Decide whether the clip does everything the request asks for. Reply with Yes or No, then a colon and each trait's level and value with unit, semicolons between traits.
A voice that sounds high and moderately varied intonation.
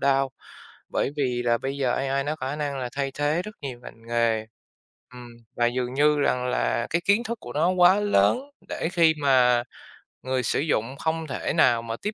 No: low, 135 Hz; average, 4.3 semitones